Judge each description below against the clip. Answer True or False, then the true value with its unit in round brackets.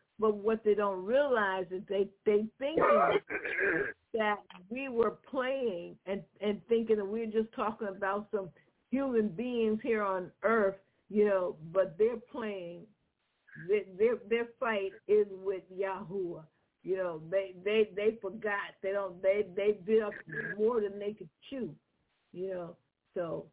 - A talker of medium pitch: False (205 Hz)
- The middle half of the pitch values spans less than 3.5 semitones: True (2.9 semitones)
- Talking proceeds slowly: False (155 wpm)